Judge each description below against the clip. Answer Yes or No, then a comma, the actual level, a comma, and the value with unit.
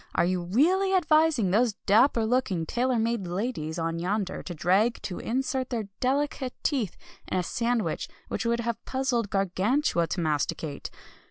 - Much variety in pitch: Yes, wide, 6.1 semitones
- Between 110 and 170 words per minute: Yes, average, 150 wpm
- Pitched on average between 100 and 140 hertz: No, high, 225 Hz